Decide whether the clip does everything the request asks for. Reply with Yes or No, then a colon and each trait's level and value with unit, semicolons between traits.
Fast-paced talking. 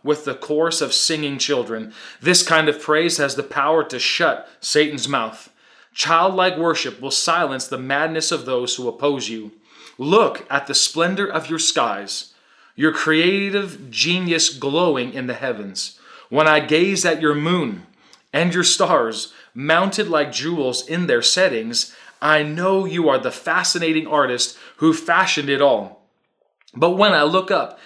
No: average, 155 wpm